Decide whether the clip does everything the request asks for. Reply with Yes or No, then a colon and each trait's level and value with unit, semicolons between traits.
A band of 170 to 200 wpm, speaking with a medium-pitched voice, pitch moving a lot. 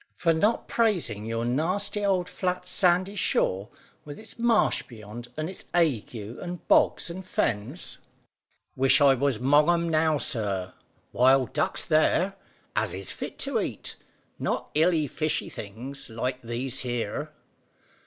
No: average, 140 wpm; medium, 150 Hz; wide, 7.1 semitones